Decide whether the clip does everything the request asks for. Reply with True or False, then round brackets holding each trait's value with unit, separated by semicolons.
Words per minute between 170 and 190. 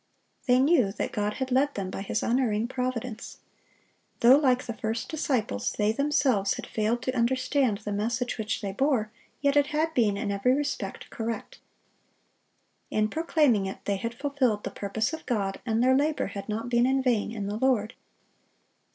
True (175 wpm)